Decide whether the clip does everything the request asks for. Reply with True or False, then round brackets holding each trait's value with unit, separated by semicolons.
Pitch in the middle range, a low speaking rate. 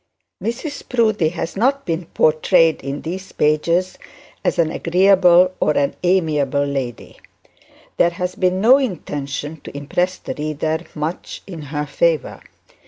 True (165 Hz; 130 wpm)